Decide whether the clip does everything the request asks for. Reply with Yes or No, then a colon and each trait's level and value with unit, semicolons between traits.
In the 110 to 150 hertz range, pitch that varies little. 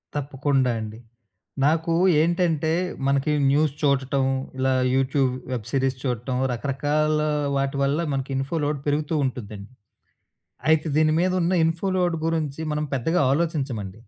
No: medium, 140 Hz; average, 3.1 semitones